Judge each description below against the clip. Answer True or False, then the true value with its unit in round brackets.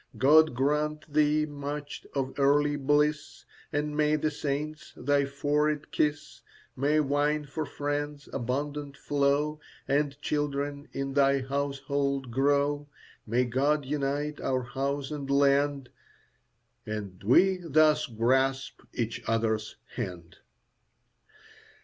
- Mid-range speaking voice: True (145 Hz)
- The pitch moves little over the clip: True (1.5 semitones)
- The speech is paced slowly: True (110 wpm)